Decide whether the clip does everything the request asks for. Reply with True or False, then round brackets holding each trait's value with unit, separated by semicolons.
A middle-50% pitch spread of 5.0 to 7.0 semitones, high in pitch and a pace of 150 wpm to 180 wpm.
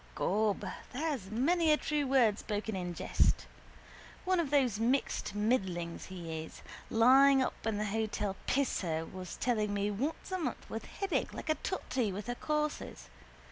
True (5.6 semitones; 225 Hz; 160 wpm)